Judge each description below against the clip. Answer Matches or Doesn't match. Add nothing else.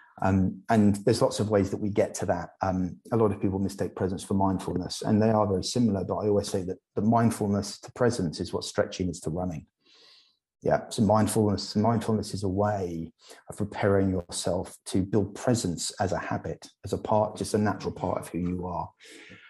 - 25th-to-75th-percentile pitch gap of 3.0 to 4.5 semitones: Doesn't match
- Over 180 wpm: Matches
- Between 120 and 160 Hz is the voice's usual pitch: Doesn't match